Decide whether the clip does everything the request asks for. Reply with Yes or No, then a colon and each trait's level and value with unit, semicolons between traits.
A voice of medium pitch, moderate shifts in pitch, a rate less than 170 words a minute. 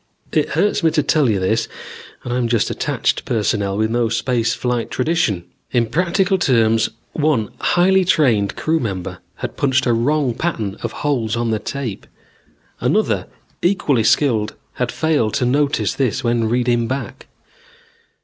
No: low, 120 Hz; average, 4.8 semitones; average, 150 wpm